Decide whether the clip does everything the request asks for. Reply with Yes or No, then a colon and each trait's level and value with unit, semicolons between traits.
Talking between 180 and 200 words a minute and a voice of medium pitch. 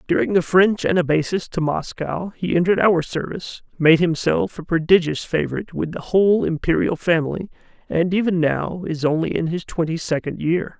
No: average, 165 wpm; medium, 170 Hz